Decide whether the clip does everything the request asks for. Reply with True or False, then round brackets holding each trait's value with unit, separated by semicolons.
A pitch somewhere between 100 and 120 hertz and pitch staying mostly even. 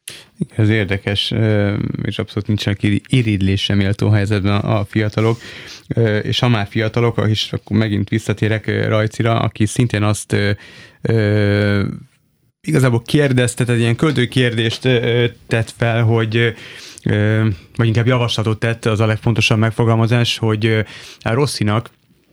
True (110 Hz; 2.0 semitones)